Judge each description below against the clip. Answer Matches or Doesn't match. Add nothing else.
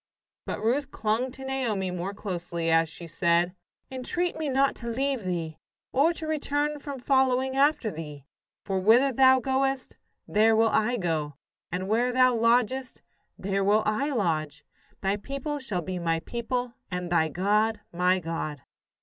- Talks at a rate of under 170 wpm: Matches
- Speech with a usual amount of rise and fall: Doesn't match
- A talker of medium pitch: Doesn't match